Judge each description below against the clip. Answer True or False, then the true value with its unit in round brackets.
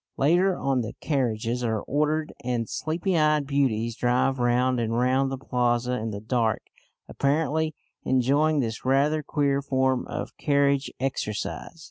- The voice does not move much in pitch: False (3.2 semitones)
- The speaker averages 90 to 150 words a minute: True (140 wpm)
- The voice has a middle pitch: False (130 Hz)